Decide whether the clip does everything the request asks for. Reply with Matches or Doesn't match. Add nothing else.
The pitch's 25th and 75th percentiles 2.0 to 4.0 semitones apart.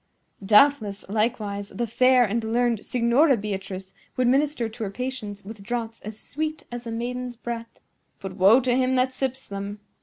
Matches